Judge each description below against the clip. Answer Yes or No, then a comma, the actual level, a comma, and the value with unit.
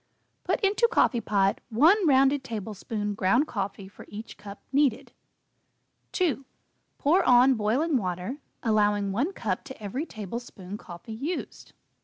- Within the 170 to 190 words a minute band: No, slow, 135 wpm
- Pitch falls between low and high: No, high, 225 Hz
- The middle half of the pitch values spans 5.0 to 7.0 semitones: Yes, average, 5.3 semitones